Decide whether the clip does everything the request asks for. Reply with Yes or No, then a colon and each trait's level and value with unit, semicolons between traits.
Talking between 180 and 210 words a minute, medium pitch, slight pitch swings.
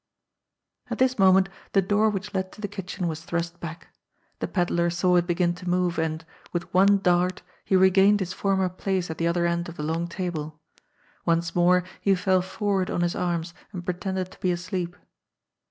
Yes: average, 190 wpm; medium, 180 Hz; narrow, 1.8 semitones